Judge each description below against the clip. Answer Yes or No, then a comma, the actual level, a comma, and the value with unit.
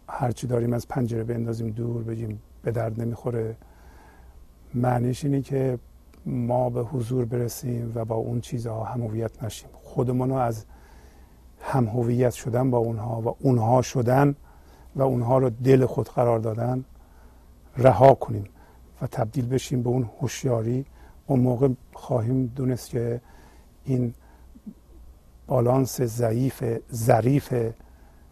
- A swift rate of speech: No, average, 120 wpm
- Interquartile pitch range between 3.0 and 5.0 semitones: No, narrow, 2.4 semitones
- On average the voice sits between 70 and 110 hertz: No, low, 120 Hz